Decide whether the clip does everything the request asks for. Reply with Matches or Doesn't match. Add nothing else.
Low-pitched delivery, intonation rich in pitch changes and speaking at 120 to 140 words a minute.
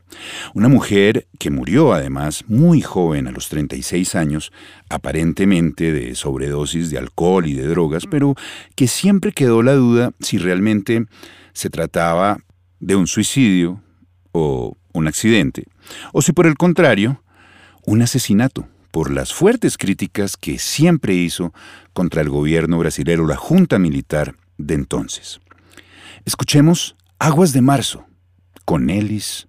Matches